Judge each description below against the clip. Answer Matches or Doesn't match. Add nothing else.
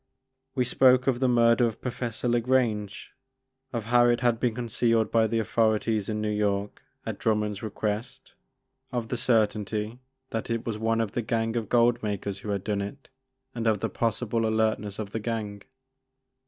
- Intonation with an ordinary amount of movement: Doesn't match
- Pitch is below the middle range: Matches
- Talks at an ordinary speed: Matches